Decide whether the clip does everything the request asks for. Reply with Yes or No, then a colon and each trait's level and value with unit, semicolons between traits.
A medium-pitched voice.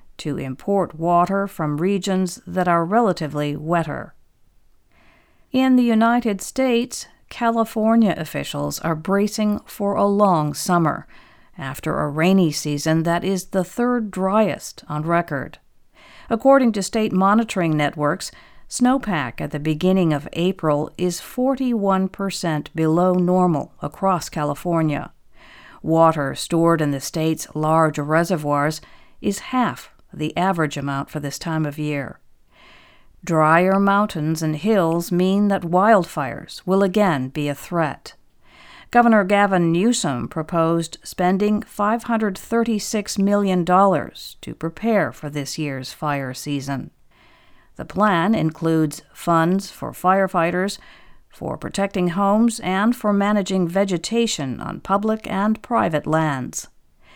Yes: medium, 180 Hz